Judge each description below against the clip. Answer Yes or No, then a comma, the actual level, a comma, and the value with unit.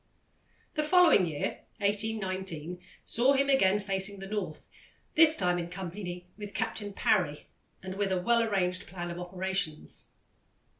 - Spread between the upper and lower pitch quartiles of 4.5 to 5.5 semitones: No, average, 3.2 semitones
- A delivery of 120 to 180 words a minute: Yes, average, 140 wpm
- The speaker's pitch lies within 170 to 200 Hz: Yes, high, 190 Hz